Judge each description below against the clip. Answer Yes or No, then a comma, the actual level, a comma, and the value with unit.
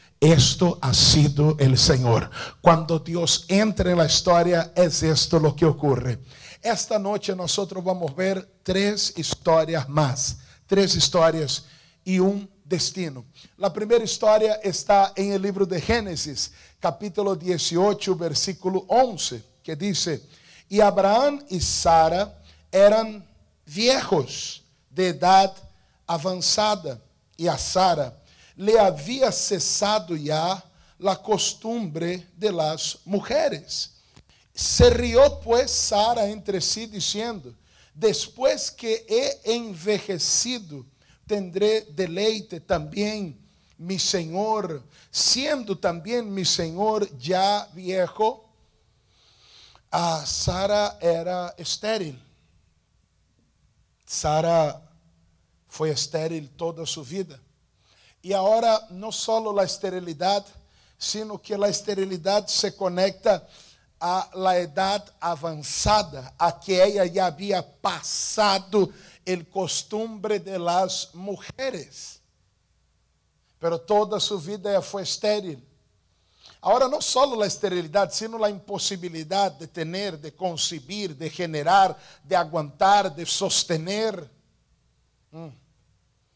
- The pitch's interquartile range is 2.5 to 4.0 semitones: No, average, 4.6 semitones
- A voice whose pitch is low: No, medium, 185 Hz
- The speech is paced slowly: Yes, slow, 105 wpm